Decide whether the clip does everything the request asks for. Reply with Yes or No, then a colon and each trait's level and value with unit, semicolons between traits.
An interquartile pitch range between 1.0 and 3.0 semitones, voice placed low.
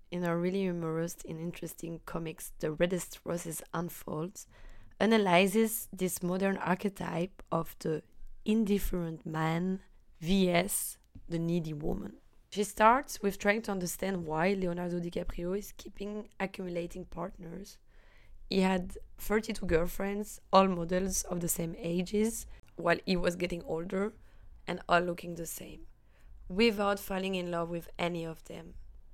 No: narrow, 2.6 semitones; medium, 175 Hz